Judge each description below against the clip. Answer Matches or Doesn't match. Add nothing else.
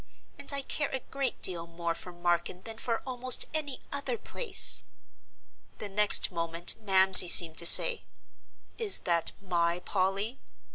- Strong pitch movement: Matches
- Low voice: Doesn't match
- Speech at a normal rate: Matches